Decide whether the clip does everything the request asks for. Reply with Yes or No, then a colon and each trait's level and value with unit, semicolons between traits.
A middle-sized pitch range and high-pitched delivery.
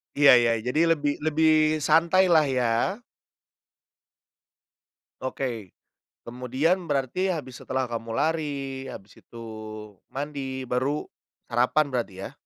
No: average, 3.7 semitones; low, 135 Hz